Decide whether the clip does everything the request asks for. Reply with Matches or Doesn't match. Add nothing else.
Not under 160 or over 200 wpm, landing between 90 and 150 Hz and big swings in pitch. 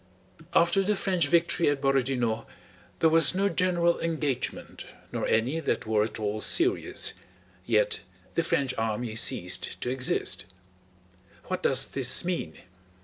Doesn't match